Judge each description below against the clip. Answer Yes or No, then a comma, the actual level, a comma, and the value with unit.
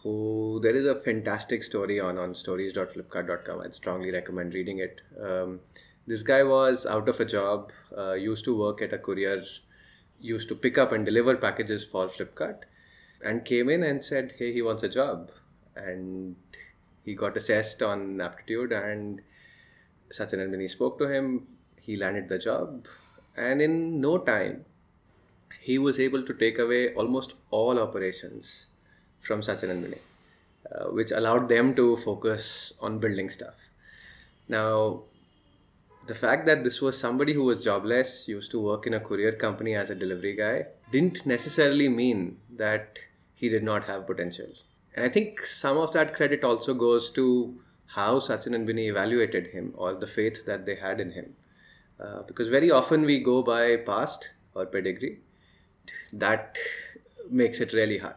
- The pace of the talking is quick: No, average, 165 wpm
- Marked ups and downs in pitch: No, average, 4.8 semitones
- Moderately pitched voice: No, low, 110 Hz